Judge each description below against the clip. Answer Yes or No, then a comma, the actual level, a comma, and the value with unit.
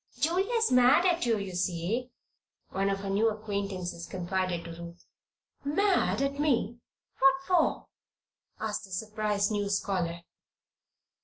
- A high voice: Yes, high, 210 Hz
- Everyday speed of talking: No, slow, 130 wpm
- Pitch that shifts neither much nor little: No, wide, 6.3 semitones